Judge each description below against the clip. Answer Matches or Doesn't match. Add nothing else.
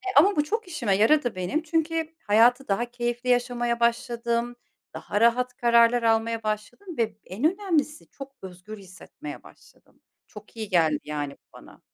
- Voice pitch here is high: Matches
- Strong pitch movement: Doesn't match